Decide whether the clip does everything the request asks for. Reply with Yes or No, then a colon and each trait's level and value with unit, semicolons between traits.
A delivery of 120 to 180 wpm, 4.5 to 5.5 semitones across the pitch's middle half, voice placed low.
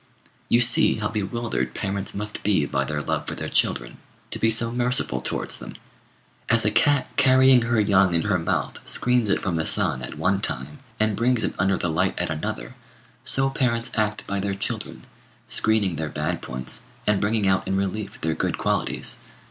No: average, 190 wpm; average, 5.1 semitones; low, 100 Hz